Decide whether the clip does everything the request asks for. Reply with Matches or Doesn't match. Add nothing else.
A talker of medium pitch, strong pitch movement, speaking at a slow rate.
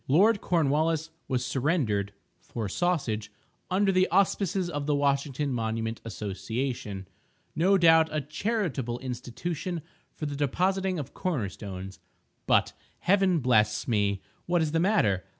Matches